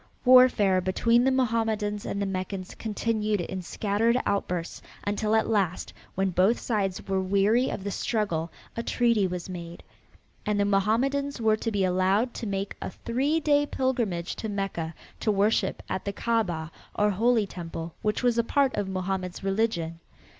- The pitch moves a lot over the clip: No, average, 3.6 semitones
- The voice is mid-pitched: No, high, 205 Hz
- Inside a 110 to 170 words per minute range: Yes, average, 165 wpm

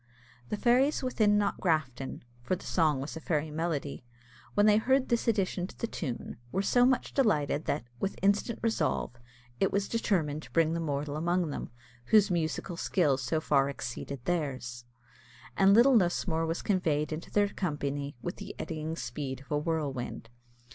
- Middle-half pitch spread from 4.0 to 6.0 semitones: Yes, wide, 5.6 semitones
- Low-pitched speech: No, medium, 165 Hz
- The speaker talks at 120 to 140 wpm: No, average, 170 wpm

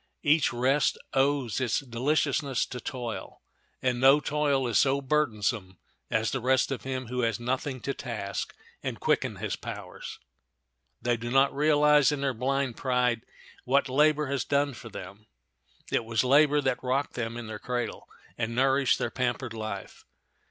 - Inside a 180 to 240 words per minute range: No, average, 160 wpm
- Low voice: Yes, low, 130 Hz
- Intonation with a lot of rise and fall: No, average, 3.0 semitones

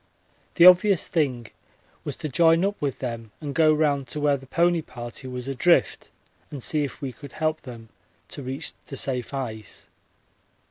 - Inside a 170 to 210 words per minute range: Yes, average, 175 wpm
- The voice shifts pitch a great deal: No, average, 3.9 semitones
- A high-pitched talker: No, medium, 140 Hz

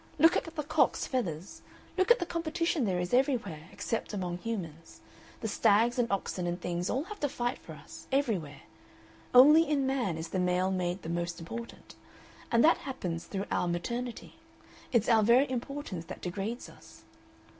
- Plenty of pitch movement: Yes, wide, 7.1 semitones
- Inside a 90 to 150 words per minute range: No, average, 175 wpm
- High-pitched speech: Yes, high, 225 Hz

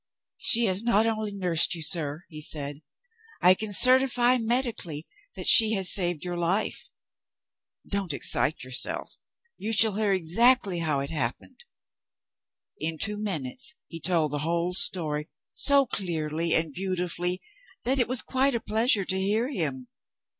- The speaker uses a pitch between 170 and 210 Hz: Yes, medium, 185 Hz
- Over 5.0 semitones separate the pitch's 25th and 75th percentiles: Yes, wide, 5.6 semitones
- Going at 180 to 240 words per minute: No, average, 145 wpm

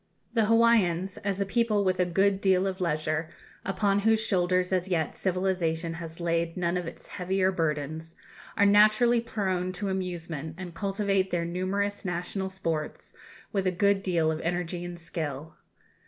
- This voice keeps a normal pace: Yes, average, 160 wpm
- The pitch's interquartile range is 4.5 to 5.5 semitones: No, average, 2.8 semitones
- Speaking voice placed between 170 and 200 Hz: Yes, medium, 185 Hz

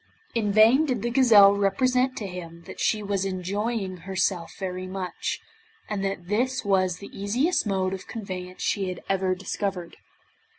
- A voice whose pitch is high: Yes, high, 195 Hz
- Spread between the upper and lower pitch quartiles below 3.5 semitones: Yes, average, 2.7 semitones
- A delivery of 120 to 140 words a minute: No, average, 160 wpm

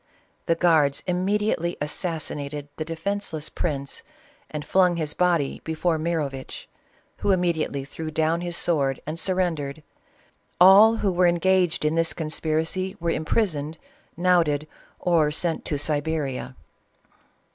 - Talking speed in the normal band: No, slow, 125 wpm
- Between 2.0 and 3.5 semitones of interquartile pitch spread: Yes, average, 2.9 semitones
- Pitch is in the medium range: Yes, medium, 160 Hz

